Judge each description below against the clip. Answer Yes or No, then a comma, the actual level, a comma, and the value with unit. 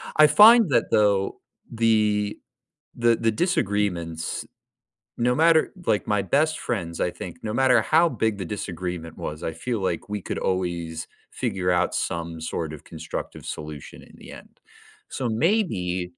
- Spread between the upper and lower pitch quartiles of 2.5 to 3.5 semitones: No, wide, 5.6 semitones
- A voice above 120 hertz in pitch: No, low, 105 Hz